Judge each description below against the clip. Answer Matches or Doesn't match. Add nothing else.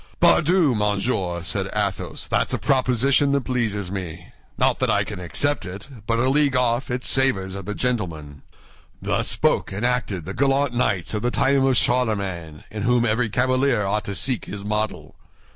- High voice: Doesn't match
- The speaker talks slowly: Doesn't match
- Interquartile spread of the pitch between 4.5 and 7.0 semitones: Matches